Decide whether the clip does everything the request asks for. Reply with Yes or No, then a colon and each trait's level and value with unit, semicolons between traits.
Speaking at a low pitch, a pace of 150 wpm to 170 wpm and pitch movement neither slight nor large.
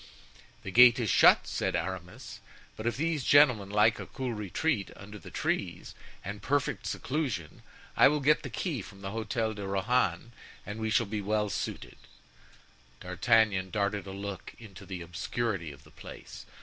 Yes: low, 105 Hz; average, 165 wpm; average, 3.7 semitones